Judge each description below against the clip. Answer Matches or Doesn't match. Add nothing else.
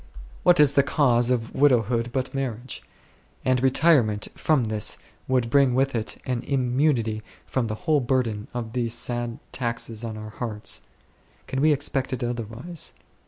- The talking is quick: Doesn't match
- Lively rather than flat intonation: Doesn't match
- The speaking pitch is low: Matches